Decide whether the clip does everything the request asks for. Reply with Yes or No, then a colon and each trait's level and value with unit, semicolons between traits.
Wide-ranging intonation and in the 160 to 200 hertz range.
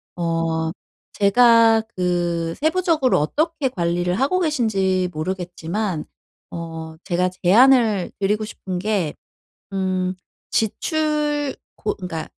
Yes: wide, 6.1 semitones; high, 190 Hz